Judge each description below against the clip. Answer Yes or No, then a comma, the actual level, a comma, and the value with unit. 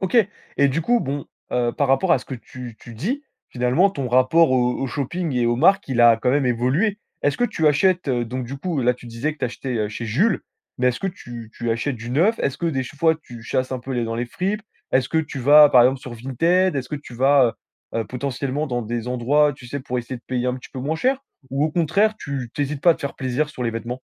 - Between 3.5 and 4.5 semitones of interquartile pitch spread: Yes, average, 4.0 semitones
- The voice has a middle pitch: No, low, 130 Hz